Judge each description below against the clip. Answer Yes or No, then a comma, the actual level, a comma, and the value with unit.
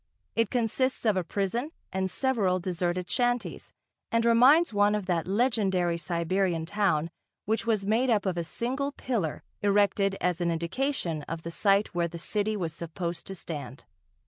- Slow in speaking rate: No, average, 165 wpm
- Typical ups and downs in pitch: Yes, average, 4.9 semitones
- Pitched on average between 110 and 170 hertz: No, high, 195 Hz